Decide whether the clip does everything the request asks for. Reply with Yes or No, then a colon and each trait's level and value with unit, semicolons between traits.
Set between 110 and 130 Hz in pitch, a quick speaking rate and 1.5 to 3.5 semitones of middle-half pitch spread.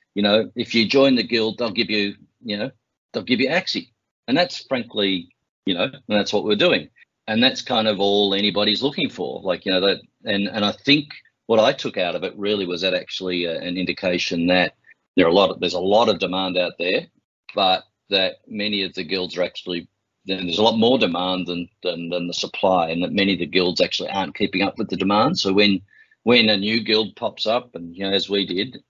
No: low, 100 Hz; fast, 235 wpm; average, 3.0 semitones